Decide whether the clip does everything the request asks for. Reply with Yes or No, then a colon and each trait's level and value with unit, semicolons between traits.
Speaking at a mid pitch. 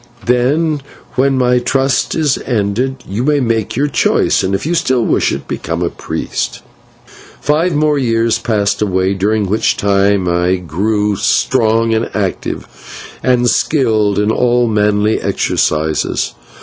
No: low, 115 Hz